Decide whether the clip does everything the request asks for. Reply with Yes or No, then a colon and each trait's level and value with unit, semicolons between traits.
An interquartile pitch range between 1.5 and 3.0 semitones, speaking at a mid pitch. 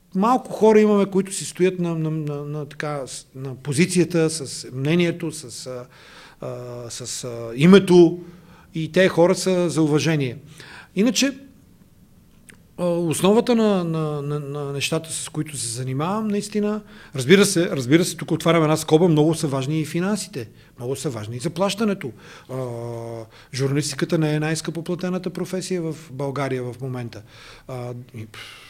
No: average, 5.0 semitones; medium, 155 Hz